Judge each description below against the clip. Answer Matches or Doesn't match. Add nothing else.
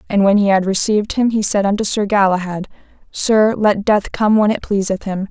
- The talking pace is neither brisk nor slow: Doesn't match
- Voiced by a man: Doesn't match